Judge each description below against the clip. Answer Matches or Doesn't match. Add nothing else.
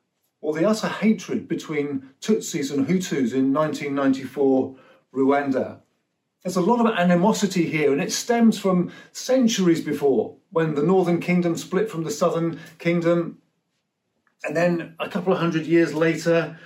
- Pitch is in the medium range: Matches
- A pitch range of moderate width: Matches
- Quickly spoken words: Doesn't match